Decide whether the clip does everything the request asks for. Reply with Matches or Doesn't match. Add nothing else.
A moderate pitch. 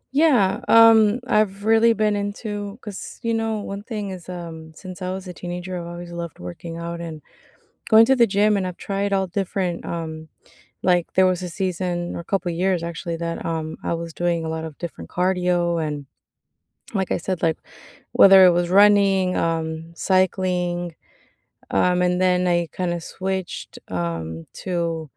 Matches